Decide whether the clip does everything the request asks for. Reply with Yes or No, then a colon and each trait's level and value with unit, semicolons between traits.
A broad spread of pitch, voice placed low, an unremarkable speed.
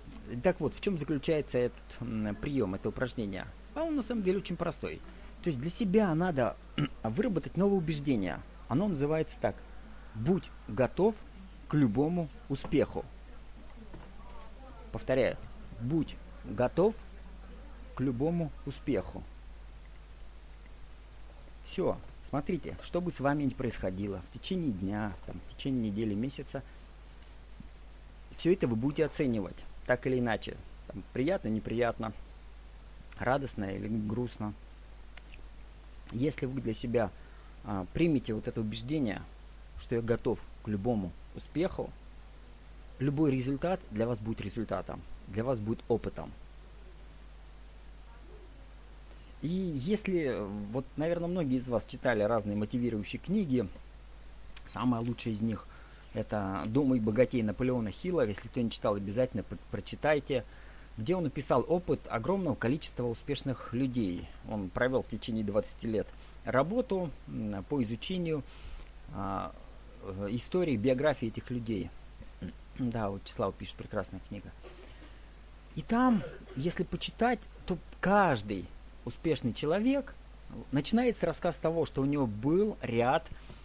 Yes: wide, 7.2 semitones; low, 120 Hz; average, 120 wpm